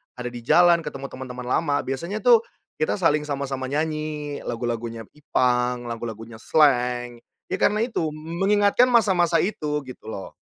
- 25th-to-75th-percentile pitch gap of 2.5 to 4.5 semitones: No, wide, 5.4 semitones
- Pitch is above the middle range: No, medium, 145 Hz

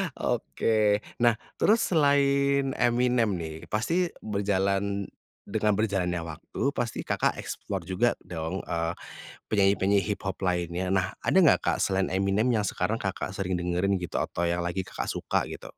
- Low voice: Yes, low, 100 Hz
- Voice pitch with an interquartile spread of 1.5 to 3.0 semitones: No, average, 4.0 semitones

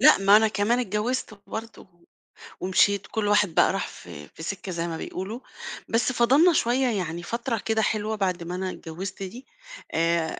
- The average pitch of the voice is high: Yes, high, 205 Hz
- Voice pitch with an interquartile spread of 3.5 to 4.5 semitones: Yes, average, 4.1 semitones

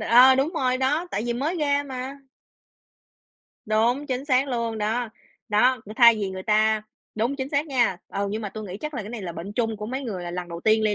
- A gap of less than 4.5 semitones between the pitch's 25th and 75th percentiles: Yes, average, 3.8 semitones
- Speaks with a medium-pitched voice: No, high, 235 Hz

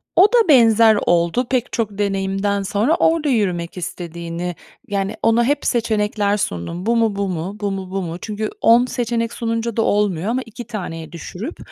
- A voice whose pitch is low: No, high, 210 Hz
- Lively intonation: No, average, 3.7 semitones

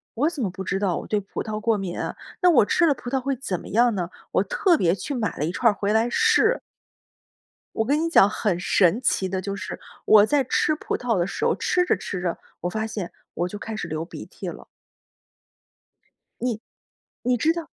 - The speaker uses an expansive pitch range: Yes, wide, 6.0 semitones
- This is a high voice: Yes, high, 220 Hz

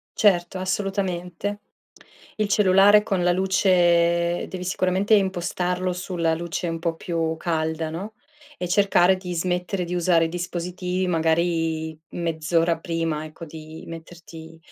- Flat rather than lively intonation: Yes, narrow, 2.0 semitones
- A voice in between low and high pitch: Yes, medium, 175 Hz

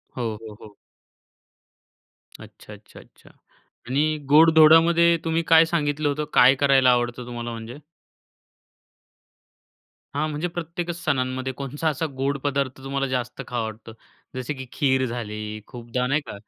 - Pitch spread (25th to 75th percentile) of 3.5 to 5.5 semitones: Yes, average, 4.0 semitones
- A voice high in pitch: No, low, 135 Hz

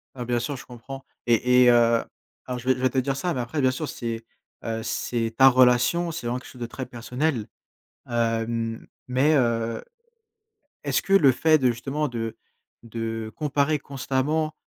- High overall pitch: No, low, 125 Hz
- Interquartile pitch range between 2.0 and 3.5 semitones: Yes, average, 2.8 semitones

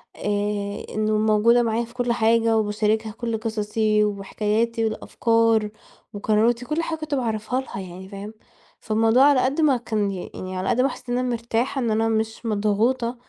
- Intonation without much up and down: Yes, narrow, 2.1 semitones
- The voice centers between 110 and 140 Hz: No, high, 225 Hz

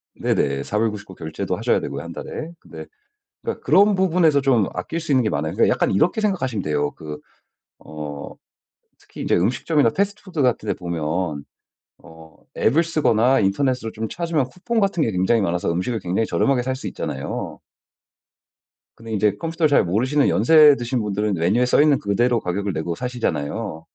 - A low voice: Yes, low, 115 Hz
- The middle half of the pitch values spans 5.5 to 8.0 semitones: No, wide, 8.4 semitones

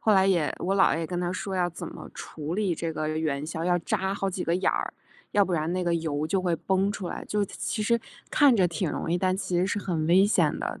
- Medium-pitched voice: Yes, medium, 180 Hz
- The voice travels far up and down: No, average, 2.8 semitones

